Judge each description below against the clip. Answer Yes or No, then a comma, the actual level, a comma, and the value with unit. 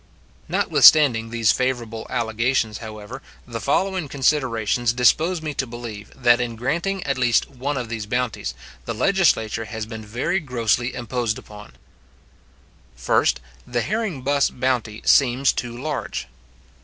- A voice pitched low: Yes, low, 120 Hz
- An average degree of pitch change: Yes, average, 3.5 semitones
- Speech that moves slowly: Yes, slow, 130 wpm